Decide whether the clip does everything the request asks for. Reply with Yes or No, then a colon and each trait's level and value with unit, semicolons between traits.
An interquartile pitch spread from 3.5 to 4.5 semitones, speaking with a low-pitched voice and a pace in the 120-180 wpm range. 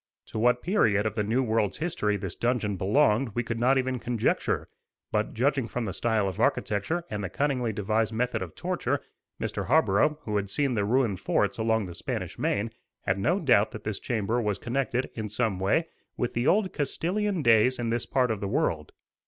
No: average, 3.9 semitones; low, 115 Hz; average, 200 wpm